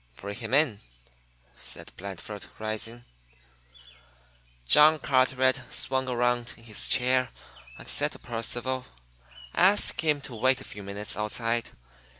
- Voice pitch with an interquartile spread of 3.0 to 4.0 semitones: Yes, average, 3.3 semitones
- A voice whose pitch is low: Yes, low, 120 Hz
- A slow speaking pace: Yes, slow, 125 wpm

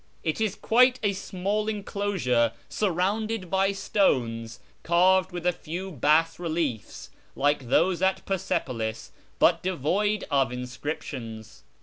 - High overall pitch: No, medium, 175 Hz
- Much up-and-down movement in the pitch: Yes, wide, 6.6 semitones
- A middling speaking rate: No, slow, 115 wpm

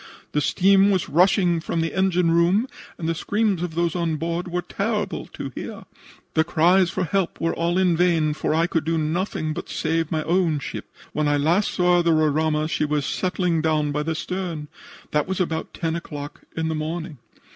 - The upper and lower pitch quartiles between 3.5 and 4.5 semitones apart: No, narrow, 2.4 semitones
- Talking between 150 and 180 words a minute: No, average, 200 wpm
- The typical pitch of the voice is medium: Yes, medium, 165 Hz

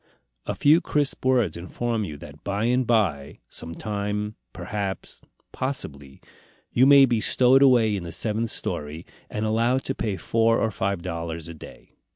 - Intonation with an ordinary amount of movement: No, wide, 6.0 semitones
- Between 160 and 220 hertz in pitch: No, low, 105 Hz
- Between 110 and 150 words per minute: No, average, 165 wpm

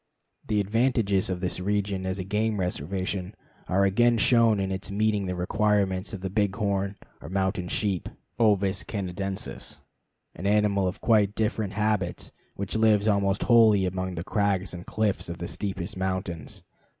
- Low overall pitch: Yes, low, 100 Hz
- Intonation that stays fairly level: Yes, narrow, 2.1 semitones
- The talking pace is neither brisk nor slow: Yes, average, 155 wpm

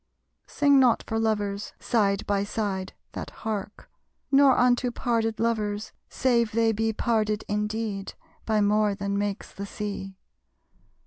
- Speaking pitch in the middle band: No, high, 215 Hz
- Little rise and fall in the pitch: Yes, narrow, 2.1 semitones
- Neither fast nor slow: No, slow, 130 wpm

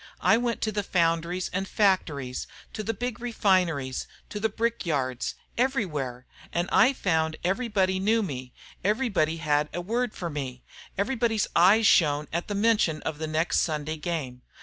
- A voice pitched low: No, medium, 180 Hz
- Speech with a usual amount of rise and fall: No, wide, 6.0 semitones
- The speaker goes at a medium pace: Yes, average, 160 wpm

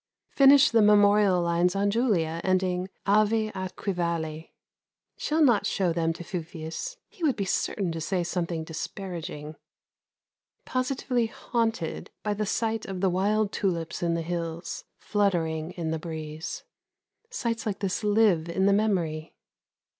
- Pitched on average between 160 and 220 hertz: Yes, medium, 185 Hz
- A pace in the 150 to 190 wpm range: No, average, 140 wpm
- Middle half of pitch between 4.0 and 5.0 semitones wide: Yes, average, 4.3 semitones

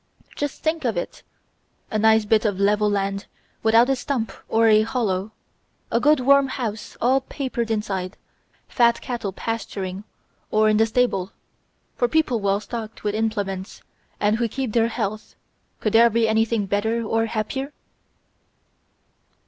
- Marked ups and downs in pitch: No, narrow, 2.5 semitones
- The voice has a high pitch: Yes, high, 220 Hz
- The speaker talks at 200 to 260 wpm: No, average, 150 wpm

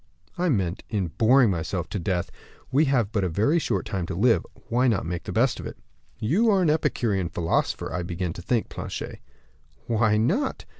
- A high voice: No, low, 105 Hz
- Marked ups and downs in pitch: Yes, wide, 6.3 semitones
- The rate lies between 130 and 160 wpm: No, average, 195 wpm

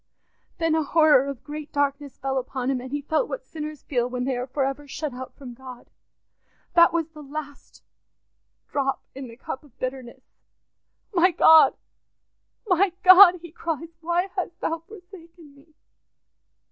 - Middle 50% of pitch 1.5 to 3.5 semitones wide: No, average, 3.9 semitones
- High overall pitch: Yes, very high, 295 Hz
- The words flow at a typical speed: Yes, average, 160 wpm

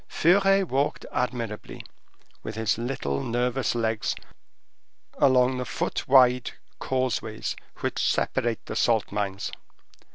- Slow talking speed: Yes, slow, 105 wpm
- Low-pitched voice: Yes, low, 125 Hz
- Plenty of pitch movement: No, average, 2.9 semitones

